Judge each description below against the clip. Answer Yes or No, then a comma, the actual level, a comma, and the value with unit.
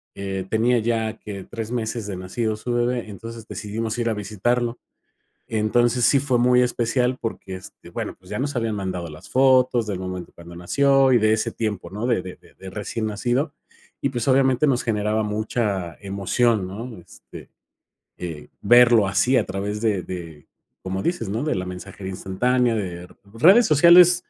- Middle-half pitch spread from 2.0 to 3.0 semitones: No, average, 4.1 semitones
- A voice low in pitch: Yes, low, 110 Hz